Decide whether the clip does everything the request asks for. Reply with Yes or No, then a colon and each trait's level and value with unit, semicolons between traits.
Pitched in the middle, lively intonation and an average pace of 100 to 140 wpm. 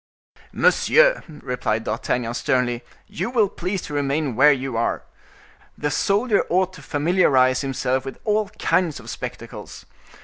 Yes: medium, 145 Hz; wide, 6.6 semitones; slow, 135 wpm